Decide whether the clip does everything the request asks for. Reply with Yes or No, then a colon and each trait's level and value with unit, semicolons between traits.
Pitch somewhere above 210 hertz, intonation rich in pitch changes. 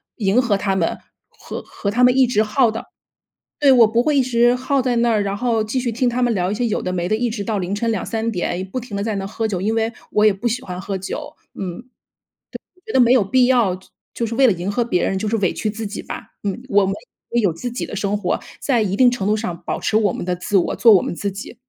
No: high, 220 Hz; average, 3.7 semitones